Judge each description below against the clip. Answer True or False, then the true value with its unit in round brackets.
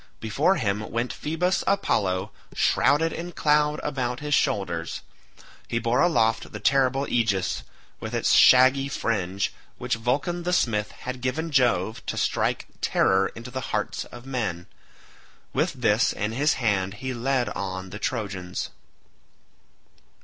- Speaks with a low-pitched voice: True (120 Hz)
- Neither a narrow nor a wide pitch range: True (4.9 semitones)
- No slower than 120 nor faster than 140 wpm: True (135 wpm)